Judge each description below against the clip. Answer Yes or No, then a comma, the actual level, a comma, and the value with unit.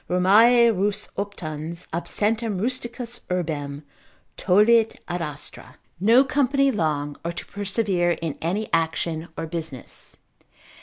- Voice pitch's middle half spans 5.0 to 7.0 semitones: Yes, wide, 5.6 semitones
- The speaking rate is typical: No, slow, 110 wpm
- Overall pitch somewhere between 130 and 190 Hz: Yes, medium, 185 Hz